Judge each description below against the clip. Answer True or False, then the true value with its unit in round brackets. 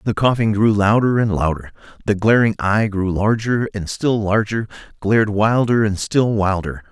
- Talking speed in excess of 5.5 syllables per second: False (4.6 syllables/s)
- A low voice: True (105 Hz)